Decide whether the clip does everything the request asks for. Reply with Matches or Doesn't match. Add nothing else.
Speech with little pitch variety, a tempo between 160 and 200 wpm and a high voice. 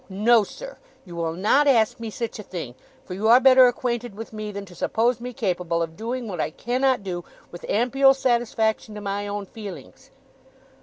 Doesn't match